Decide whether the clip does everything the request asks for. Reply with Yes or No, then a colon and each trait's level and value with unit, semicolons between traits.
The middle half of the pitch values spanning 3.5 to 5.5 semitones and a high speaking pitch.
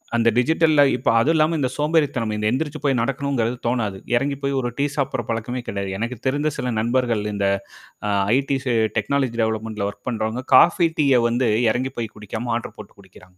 No: average, 4.0 semitones; low, 125 Hz